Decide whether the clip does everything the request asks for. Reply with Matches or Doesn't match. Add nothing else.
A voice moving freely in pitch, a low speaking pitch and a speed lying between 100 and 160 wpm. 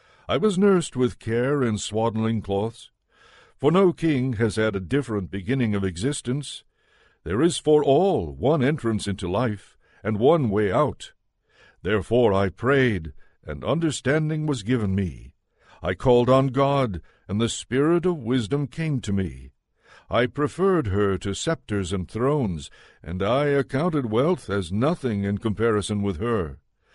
Matches